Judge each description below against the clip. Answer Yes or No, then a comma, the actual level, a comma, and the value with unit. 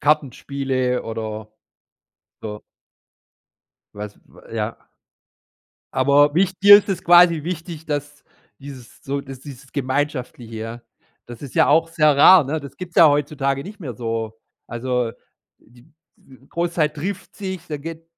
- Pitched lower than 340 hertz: Yes, medium, 140 Hz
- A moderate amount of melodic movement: Yes, average, 4.7 semitones